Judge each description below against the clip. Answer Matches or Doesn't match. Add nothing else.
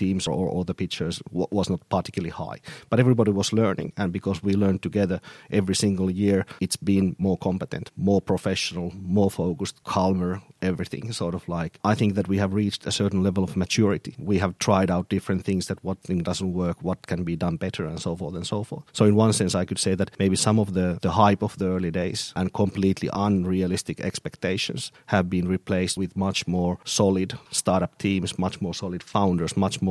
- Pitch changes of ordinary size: Doesn't match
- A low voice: Matches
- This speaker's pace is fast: Matches